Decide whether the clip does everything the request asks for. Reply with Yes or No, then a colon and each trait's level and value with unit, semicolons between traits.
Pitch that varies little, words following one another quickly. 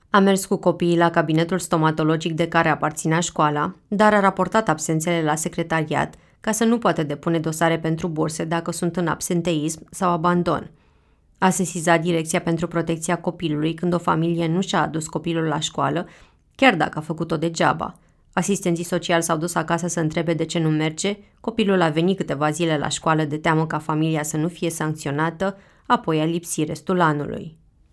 Yes: narrow, 1.9 semitones; fast, 175 wpm